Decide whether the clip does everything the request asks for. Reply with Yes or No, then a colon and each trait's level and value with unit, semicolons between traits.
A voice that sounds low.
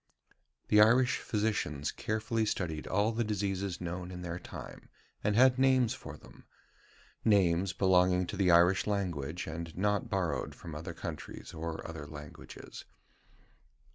Yes: very low, 95 Hz